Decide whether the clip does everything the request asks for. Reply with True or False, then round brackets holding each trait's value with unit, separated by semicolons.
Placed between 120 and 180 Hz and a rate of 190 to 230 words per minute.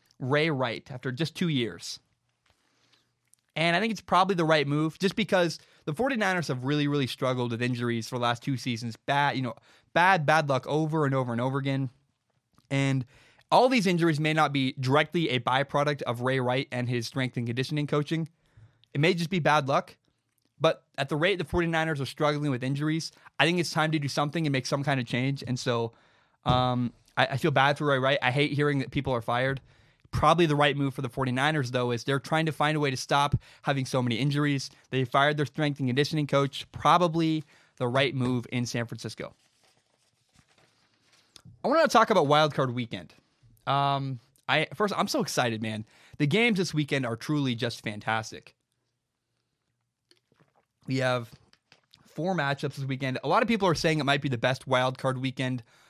True (140 Hz; 195 wpm)